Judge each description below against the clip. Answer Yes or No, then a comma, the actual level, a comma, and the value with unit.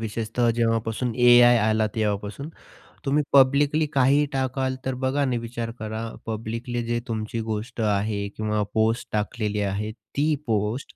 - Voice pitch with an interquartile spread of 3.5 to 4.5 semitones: No, average, 3.0 semitones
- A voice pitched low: Yes, low, 115 Hz